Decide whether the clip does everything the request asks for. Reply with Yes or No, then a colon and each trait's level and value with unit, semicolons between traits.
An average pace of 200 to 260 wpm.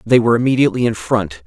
Yes: fast, 205 wpm